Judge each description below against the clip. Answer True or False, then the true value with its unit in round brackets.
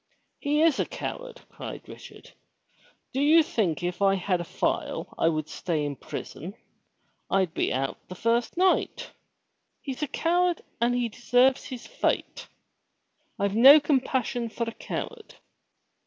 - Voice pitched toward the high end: True (240 Hz)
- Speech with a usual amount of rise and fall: False (7.9 semitones)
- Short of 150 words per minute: True (140 wpm)